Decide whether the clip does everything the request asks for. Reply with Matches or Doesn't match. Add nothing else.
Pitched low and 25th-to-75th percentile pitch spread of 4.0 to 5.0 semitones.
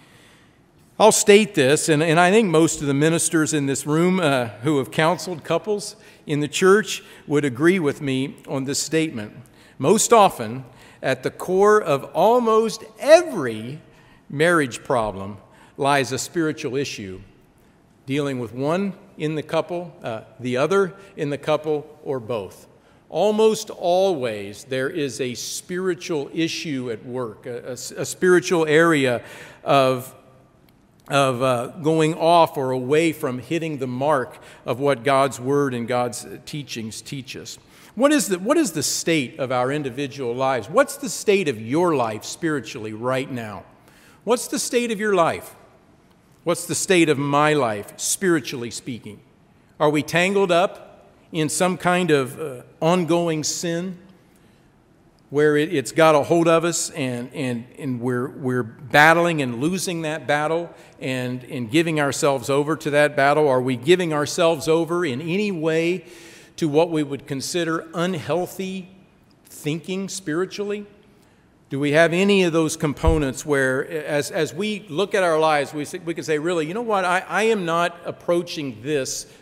Doesn't match